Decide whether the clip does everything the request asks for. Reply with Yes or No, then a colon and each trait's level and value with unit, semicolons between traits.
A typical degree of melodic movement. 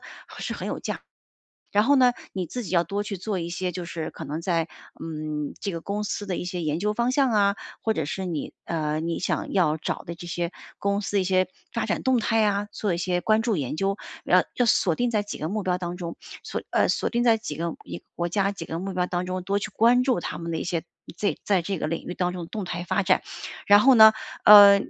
Yes: average, 3.5 semitones